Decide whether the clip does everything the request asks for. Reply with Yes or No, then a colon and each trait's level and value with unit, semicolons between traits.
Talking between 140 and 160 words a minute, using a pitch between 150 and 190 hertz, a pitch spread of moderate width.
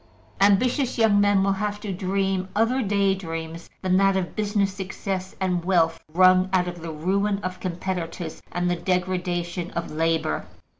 No: average, 155 wpm; medium, 185 Hz; narrow, 2.2 semitones